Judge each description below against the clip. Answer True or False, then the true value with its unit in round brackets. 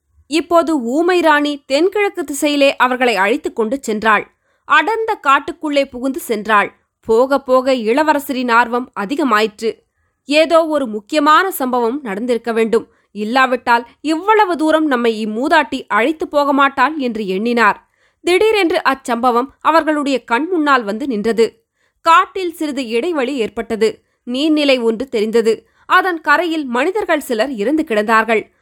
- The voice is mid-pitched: False (270 Hz)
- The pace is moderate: True (115 wpm)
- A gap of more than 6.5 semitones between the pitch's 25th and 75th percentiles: False (5.1 semitones)